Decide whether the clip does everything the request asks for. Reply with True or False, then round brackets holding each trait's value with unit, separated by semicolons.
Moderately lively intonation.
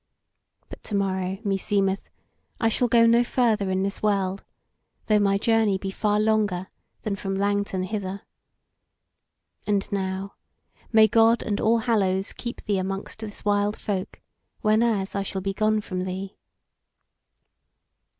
False (2.0 semitones)